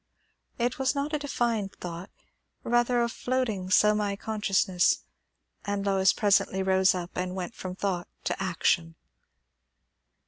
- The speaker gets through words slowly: Yes, slow, 130 wpm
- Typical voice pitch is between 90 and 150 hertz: No, high, 200 Hz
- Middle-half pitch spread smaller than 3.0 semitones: No, average, 4.1 semitones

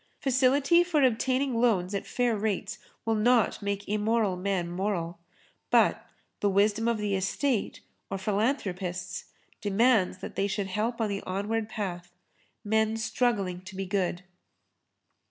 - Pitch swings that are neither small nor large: Yes, average, 3.3 semitones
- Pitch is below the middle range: No, high, 205 Hz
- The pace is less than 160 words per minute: Yes, slow, 135 wpm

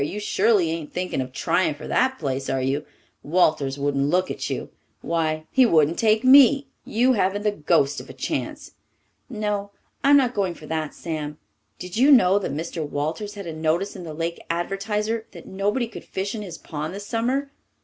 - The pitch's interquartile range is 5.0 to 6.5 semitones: Yes, wide, 5.5 semitones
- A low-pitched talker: No, medium, 185 Hz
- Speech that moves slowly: No, average, 190 wpm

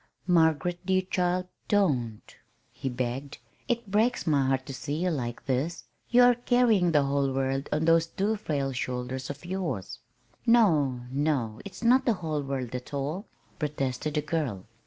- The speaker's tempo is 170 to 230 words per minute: No, average, 160 wpm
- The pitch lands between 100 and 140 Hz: No, medium, 150 Hz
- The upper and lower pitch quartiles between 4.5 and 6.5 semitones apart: Yes, wide, 5.6 semitones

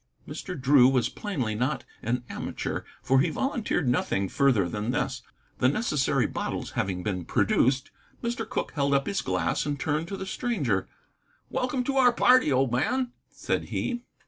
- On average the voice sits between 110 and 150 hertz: Yes, medium, 140 Hz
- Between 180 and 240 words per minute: No, average, 165 wpm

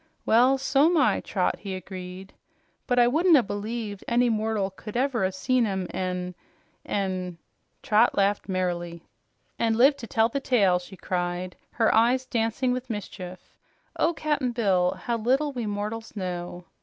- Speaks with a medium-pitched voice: No, high, 215 Hz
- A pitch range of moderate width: Yes, average, 4.9 semitones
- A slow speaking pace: No, average, 160 wpm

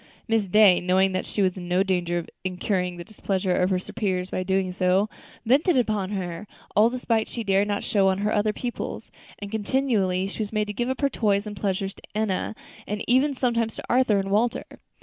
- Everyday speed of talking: No, fast, 215 wpm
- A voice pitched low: No, high, 200 Hz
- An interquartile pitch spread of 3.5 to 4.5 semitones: No, average, 2.9 semitones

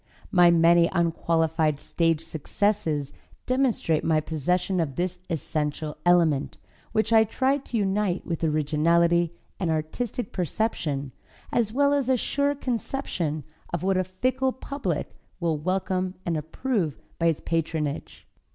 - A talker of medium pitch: Yes, medium, 170 Hz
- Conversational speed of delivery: No, slow, 130 wpm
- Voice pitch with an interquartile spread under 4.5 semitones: No, average, 5.1 semitones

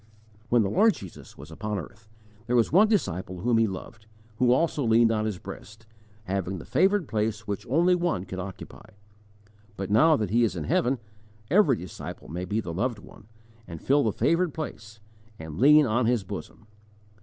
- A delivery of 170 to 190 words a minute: Yes, average, 185 wpm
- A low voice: Yes, low, 110 Hz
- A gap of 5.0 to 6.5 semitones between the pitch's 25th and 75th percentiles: Yes, wide, 5.6 semitones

